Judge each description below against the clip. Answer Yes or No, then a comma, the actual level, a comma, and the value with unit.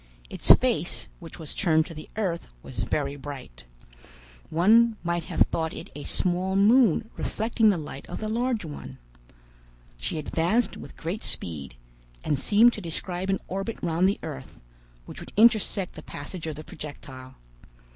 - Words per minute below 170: Yes, average, 160 wpm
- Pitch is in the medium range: Yes, medium, 170 Hz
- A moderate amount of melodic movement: No, wide, 5.8 semitones